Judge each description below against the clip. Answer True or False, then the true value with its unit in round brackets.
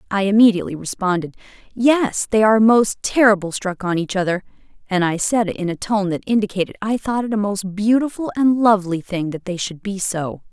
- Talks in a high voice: True (200 Hz)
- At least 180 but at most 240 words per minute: True (200 wpm)